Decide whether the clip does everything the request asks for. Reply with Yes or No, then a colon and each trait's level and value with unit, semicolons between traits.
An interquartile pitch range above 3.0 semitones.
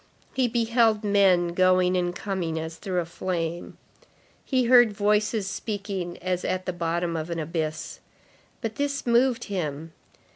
Yes: average, 4.3 semitones